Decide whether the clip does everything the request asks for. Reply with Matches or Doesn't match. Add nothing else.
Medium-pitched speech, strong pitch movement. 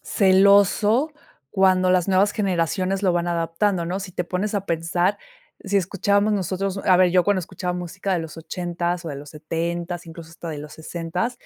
Doesn't match